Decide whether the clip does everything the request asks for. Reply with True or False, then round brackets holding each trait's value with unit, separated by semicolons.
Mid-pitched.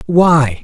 True (150 Hz)